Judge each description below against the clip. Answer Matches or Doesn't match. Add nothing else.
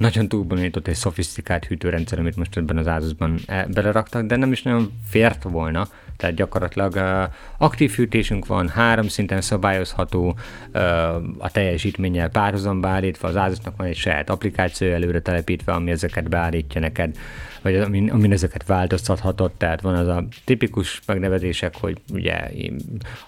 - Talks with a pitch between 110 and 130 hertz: Doesn't match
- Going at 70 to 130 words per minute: Doesn't match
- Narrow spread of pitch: Doesn't match